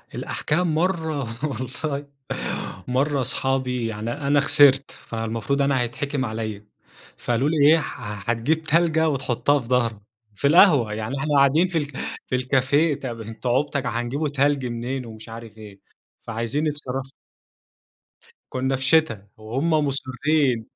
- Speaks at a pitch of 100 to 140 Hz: Yes, low, 135 Hz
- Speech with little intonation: No, average, 3.8 semitones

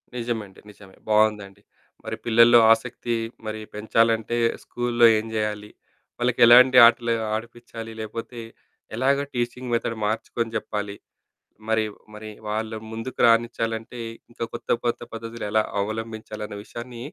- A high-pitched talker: No, low, 115 Hz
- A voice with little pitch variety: Yes, narrow, 1.6 semitones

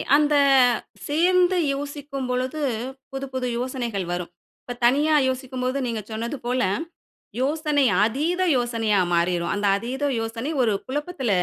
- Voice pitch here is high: Yes, very high, 255 Hz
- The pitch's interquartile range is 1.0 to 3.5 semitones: No, average, 4.1 semitones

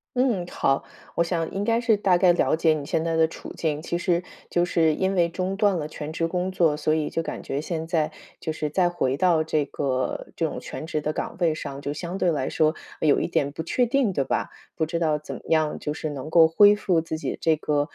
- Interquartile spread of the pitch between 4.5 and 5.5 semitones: No, average, 2.7 semitones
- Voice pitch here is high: No, medium, 165 Hz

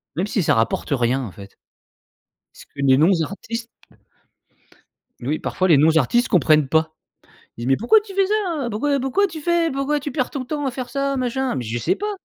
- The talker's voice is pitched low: No, high, 240 Hz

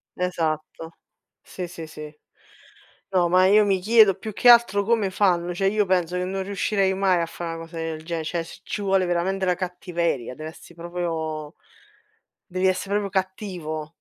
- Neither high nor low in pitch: Yes, medium, 180 Hz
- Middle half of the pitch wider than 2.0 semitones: Yes, average, 2.7 semitones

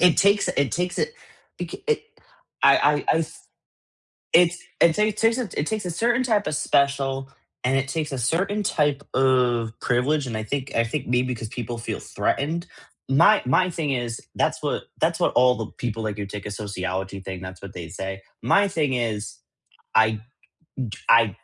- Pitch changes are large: Yes, wide, 6.8 semitones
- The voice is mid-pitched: No, low, 130 Hz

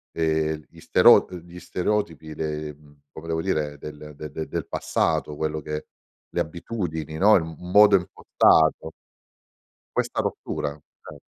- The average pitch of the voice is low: Yes, very low, 80 Hz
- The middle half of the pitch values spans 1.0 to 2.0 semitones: No, narrow, 2.4 semitones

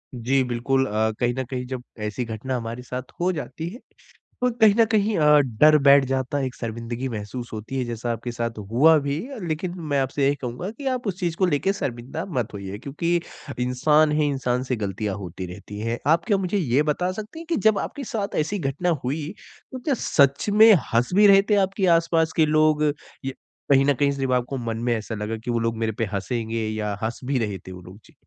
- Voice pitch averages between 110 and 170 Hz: Yes, low, 135 Hz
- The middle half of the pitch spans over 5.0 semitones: Yes, wide, 5.6 semitones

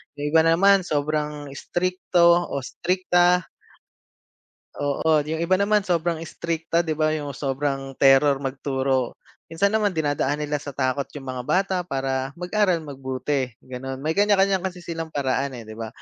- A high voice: No, medium, 150 Hz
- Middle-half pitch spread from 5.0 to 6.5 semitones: No, average, 4.4 semitones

